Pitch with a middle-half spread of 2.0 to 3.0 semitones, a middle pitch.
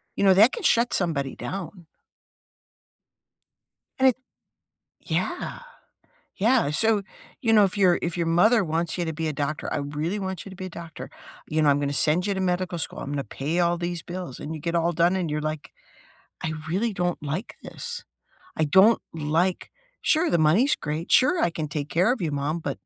No: average, 3.7 semitones; medium, 170 Hz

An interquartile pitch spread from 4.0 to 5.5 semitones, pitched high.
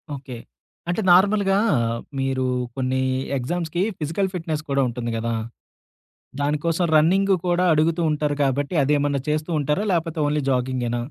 No: average, 4.6 semitones; medium, 150 Hz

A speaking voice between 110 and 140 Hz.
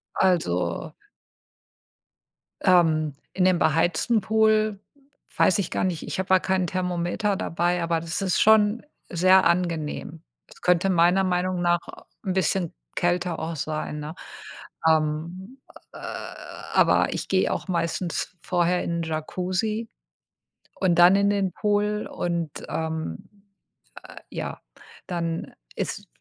No: medium, 175 Hz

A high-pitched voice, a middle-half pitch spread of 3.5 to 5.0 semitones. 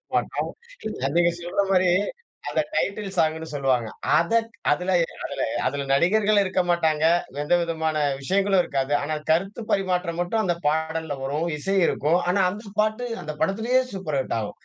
No: medium, 175 Hz; average, 4.2 semitones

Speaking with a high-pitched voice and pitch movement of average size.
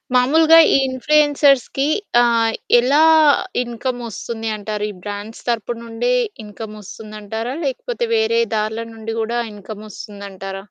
Yes: high, 225 Hz; average, 3.7 semitones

